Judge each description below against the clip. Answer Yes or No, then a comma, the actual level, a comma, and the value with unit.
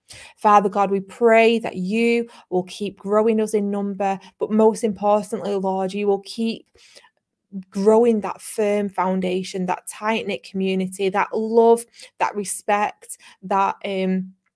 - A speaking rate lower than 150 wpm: Yes, slow, 135 wpm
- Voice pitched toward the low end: No, high, 205 Hz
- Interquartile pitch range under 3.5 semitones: Yes, narrow, 2.6 semitones